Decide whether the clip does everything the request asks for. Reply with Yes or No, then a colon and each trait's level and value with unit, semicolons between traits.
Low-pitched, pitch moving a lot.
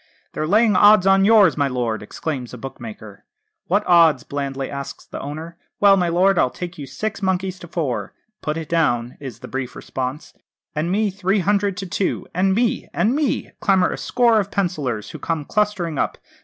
No: medium, 170 Hz; wide, 6.1 semitones